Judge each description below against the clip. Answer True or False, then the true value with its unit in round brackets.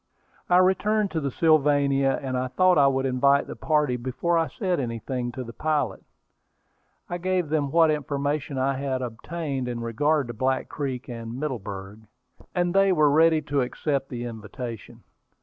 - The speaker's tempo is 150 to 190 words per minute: True (165 wpm)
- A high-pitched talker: False (140 Hz)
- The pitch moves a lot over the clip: False (4.0 semitones)